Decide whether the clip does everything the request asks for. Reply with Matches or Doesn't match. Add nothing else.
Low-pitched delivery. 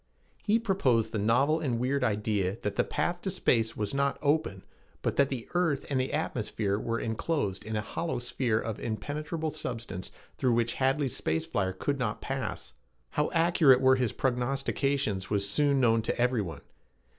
Matches